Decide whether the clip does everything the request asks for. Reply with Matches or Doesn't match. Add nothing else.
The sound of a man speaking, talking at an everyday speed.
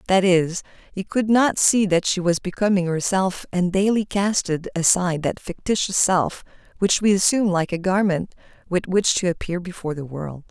Doesn't match